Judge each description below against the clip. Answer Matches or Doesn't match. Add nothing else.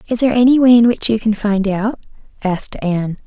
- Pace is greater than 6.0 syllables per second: Matches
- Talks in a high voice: Matches